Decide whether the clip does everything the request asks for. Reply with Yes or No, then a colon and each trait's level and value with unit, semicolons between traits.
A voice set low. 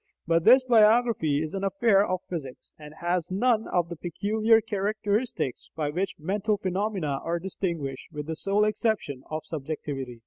No: medium, 185 Hz